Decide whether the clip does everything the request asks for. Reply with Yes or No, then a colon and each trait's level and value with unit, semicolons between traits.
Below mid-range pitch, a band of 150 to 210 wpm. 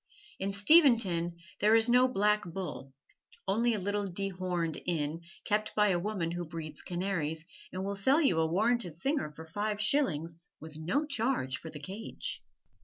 No: high, 195 Hz; average, 165 wpm